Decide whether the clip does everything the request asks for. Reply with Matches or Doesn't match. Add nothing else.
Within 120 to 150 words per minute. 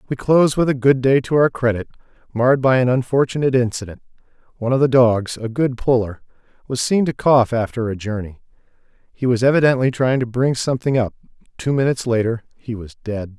Doesn't match